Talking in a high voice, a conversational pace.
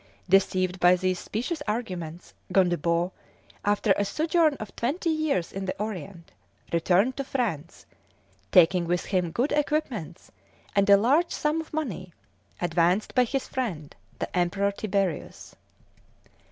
No: high, 195 Hz; slow, 130 wpm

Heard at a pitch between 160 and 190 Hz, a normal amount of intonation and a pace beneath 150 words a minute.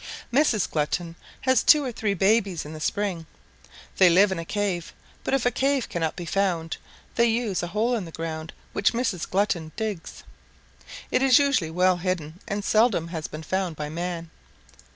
No: medium, 185 Hz; average, 5.0 semitones; average, 180 wpm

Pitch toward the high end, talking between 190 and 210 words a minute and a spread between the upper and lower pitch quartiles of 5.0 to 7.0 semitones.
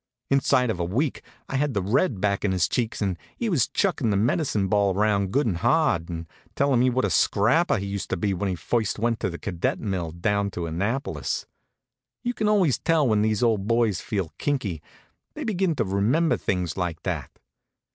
No: low, 105 Hz; fast, 205 wpm; wide, 5.6 semitones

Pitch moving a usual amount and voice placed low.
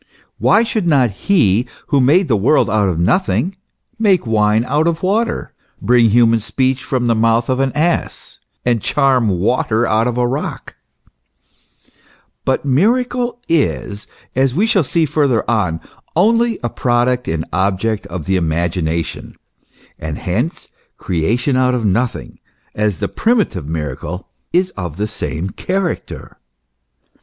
No: wide, 7.7 semitones; low, 120 Hz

